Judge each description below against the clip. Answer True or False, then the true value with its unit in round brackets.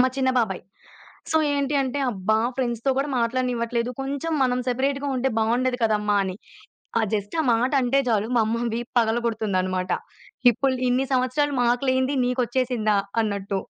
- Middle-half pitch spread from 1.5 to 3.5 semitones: True (2.9 semitones)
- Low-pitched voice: False (245 Hz)